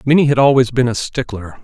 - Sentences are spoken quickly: Yes, fast, 220 wpm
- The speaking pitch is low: Yes, low, 130 Hz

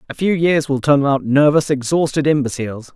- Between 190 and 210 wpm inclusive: Yes, fast, 205 wpm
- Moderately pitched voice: Yes, medium, 145 Hz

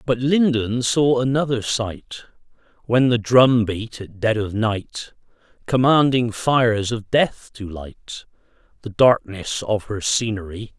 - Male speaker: Yes, male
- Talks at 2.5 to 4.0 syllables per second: Yes, 3.8 syllables/s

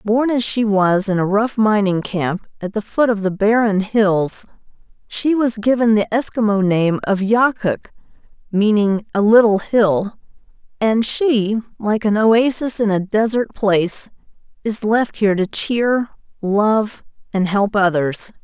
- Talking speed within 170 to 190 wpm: No, average, 150 wpm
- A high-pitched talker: Yes, high, 210 Hz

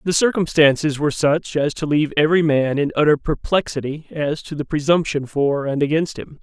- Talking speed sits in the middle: Yes, average, 185 wpm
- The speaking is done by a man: Yes, male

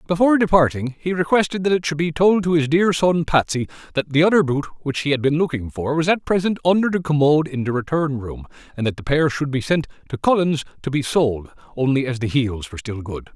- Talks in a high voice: No, medium, 150 Hz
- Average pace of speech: No, fast, 240 wpm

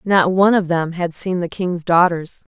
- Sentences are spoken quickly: Yes, fast, 210 wpm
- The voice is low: No, medium, 175 Hz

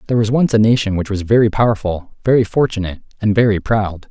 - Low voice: Yes, low, 105 Hz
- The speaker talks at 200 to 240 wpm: Yes, fast, 205 wpm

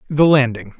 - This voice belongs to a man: Yes, male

